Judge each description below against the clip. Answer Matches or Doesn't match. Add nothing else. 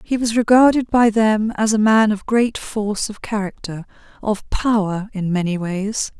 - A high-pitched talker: Matches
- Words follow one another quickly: Doesn't match